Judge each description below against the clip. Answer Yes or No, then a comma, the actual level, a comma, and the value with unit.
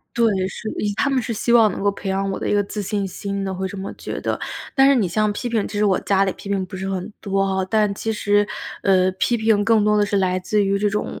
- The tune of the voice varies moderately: No, narrow, 1.8 semitones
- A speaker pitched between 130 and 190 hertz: No, high, 205 Hz